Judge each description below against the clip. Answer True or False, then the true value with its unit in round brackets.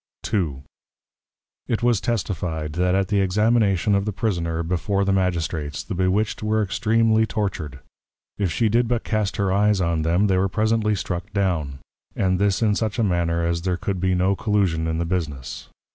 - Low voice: True (95 Hz)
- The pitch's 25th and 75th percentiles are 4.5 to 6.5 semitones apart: False (3.9 semitones)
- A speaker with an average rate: True (180 wpm)